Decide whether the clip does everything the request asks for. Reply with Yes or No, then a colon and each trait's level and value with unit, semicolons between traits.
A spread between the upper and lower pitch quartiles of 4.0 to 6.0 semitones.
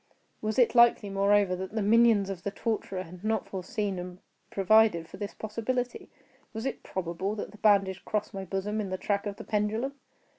No: narrow, 2.4 semitones